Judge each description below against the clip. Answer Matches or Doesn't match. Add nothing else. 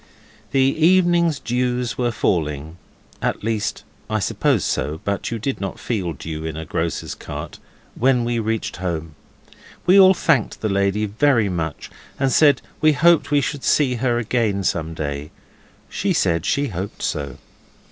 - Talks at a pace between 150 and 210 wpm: Matches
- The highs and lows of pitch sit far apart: Matches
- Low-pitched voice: Matches